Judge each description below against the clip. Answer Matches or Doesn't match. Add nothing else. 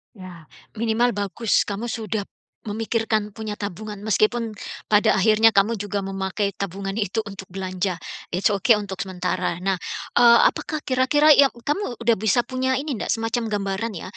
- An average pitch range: Matches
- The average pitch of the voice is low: Doesn't match